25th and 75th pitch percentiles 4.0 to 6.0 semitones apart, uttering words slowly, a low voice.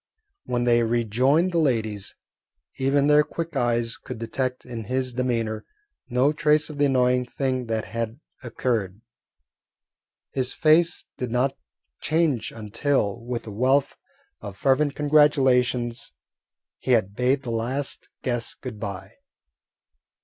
No: average, 3.2 semitones; slow, 130 wpm; low, 125 Hz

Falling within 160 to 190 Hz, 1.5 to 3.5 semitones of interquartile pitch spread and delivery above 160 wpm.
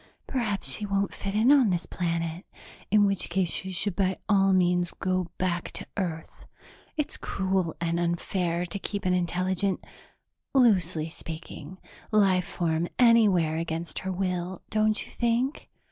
No: medium, 185 Hz; average, 2.8 semitones; average, 145 wpm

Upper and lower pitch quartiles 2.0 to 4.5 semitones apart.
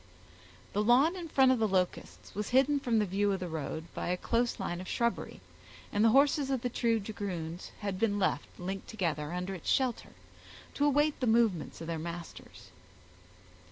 No: wide, 5.5 semitones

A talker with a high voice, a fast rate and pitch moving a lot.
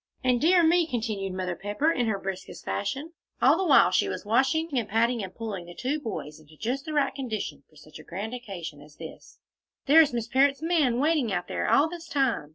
Yes: high, 235 Hz; fast, 220 wpm; wide, 7.1 semitones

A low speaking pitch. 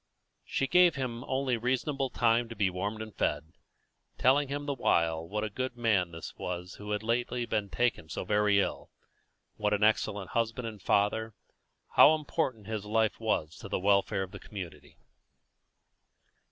Yes: low, 110 Hz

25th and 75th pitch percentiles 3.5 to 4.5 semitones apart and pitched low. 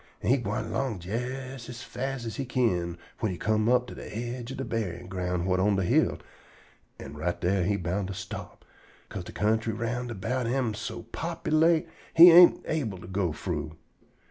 No: average, 5.2 semitones; low, 110 Hz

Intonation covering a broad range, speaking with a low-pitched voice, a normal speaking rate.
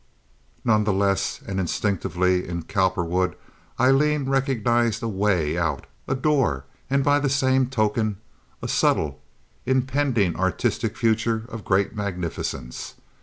No: wide, 5.9 semitones; low, 105 Hz; slow, 115 wpm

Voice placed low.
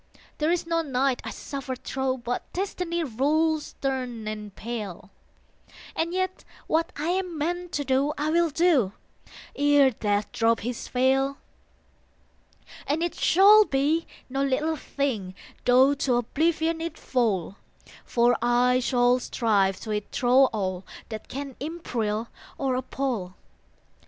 No: very high, 265 Hz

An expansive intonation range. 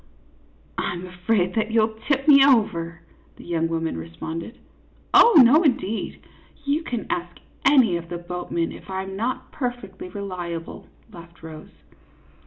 Yes: wide, 6.0 semitones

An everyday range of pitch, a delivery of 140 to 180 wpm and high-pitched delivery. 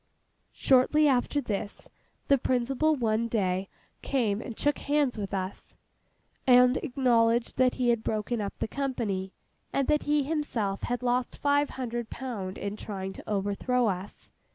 Yes: average, 4.4 semitones; average, 150 wpm; high, 240 Hz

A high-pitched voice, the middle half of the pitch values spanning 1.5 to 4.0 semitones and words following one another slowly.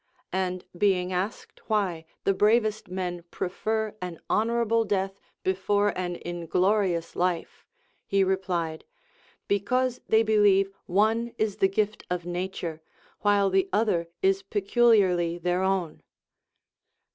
Yes: high, 195 Hz; average, 2.9 semitones; slow, 120 wpm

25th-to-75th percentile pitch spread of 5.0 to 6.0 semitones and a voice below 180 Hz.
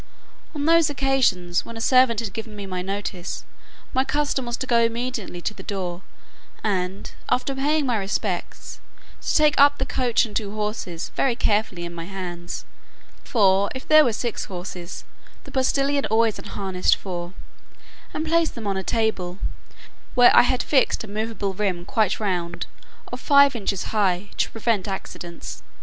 No: average, 5.3 semitones; high, 215 Hz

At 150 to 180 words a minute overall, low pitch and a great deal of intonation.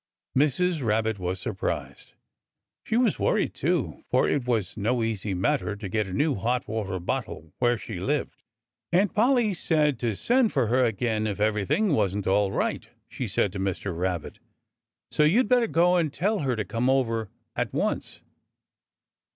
Yes: average, 165 wpm; low, 115 Hz; wide, 7.1 semitones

